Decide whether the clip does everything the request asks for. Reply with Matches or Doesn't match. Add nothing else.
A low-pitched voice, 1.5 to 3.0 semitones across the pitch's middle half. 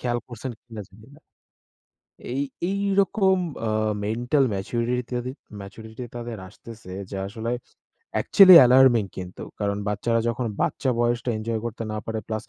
Matches